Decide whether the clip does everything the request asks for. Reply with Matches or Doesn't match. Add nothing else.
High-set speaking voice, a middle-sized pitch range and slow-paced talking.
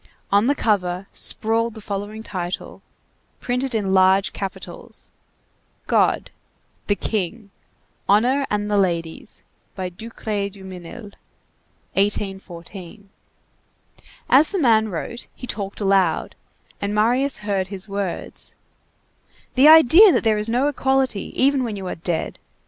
Matches